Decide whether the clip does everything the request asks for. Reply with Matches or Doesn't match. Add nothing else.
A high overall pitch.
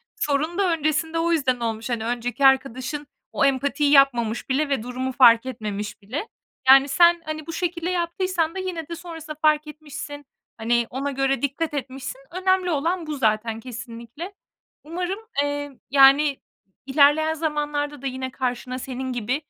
Matches